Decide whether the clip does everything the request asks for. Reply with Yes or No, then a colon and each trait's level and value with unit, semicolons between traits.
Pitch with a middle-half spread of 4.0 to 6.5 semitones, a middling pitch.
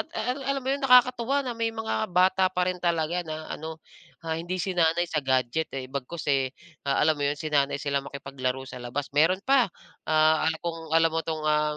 Yes: average, 4.3 semitones; medium, 160 Hz